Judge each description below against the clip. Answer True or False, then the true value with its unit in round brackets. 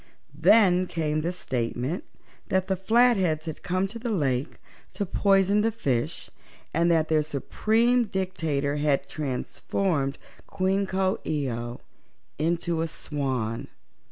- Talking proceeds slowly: True (125 wpm)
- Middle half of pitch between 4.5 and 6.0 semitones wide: True (5.0 semitones)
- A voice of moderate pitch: True (170 Hz)